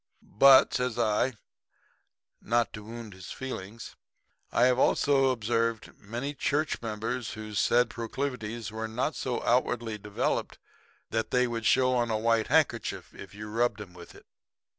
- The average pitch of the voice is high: No, low, 115 Hz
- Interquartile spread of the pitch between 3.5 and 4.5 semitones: No, narrow, 2.6 semitones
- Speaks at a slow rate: No, average, 150 wpm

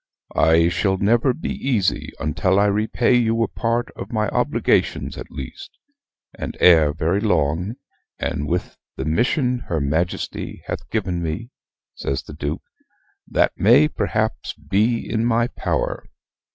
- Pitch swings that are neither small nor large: No, wide, 6.2 semitones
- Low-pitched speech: Yes, low, 100 Hz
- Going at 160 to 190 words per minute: No, average, 140 wpm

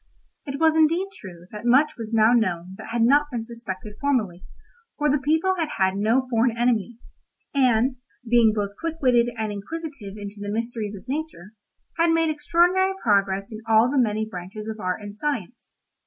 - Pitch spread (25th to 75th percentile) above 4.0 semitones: Yes, wide, 5.5 semitones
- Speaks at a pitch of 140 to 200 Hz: No, high, 230 Hz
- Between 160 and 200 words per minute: Yes, average, 180 wpm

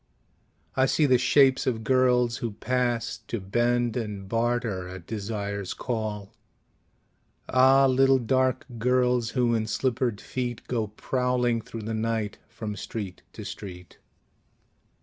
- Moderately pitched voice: No, low, 120 Hz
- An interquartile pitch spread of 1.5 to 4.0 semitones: Yes, average, 2.8 semitones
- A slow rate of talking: Yes, slow, 130 wpm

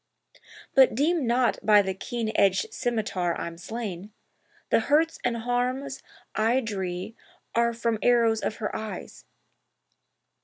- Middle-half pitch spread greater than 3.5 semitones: No, average, 3.0 semitones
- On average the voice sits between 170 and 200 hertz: No, high, 230 Hz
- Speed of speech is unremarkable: No, slow, 125 wpm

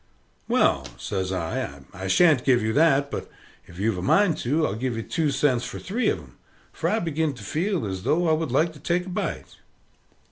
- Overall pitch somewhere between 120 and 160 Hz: Yes, medium, 140 Hz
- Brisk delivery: Yes, fast, 225 wpm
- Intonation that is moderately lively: No, wide, 7.7 semitones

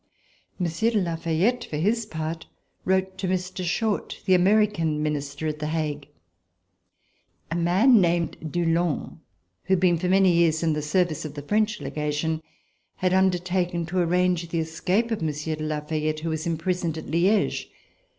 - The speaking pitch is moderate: Yes, medium, 170 Hz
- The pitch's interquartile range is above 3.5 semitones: No, average, 3.0 semitones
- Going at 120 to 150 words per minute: No, average, 165 wpm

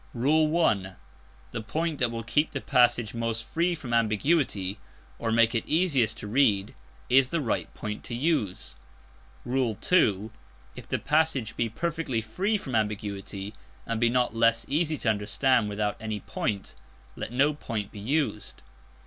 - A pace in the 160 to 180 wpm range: No, average, 150 wpm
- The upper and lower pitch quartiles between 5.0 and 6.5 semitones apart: Yes, average, 5.3 semitones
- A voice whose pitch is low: Yes, low, 115 Hz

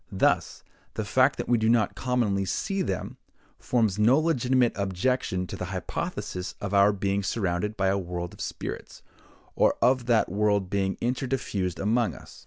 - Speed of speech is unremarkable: Yes, average, 170 wpm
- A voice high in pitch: No, low, 105 Hz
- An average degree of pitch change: Yes, average, 4.2 semitones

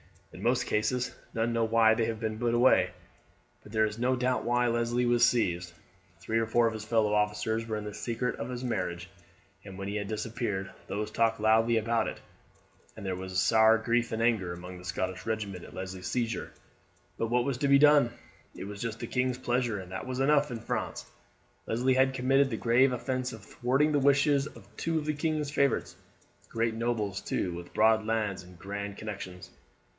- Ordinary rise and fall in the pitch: Yes, average, 3.0 semitones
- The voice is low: Yes, low, 115 Hz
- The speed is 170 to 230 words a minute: Yes, average, 200 wpm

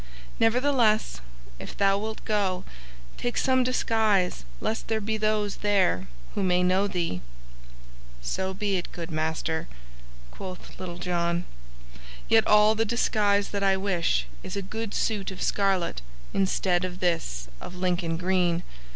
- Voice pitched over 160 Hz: Yes, high, 190 Hz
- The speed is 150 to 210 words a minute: No, average, 140 wpm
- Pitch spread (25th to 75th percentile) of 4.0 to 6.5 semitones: No, average, 3.2 semitones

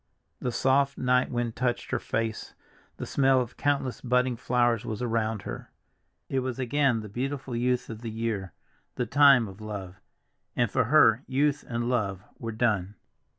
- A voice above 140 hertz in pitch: No, low, 120 Hz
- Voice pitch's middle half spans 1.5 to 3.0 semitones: Yes, average, 2.7 semitones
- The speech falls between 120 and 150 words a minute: No, average, 165 wpm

